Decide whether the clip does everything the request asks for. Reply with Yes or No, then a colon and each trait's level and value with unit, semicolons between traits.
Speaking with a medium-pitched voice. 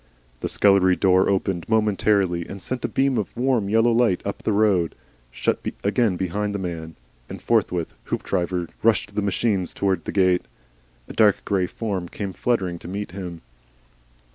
No: low, 100 Hz